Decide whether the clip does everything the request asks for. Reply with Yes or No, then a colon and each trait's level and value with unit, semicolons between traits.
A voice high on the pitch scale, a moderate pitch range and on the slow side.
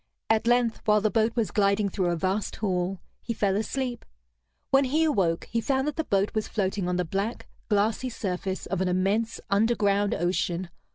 No: high, 205 Hz; average, 3.5 semitones; average, 185 wpm